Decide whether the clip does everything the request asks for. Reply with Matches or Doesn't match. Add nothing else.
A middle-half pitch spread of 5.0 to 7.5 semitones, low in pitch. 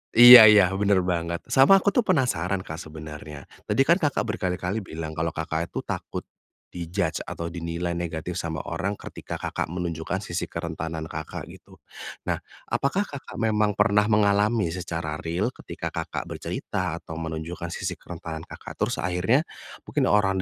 Doesn't match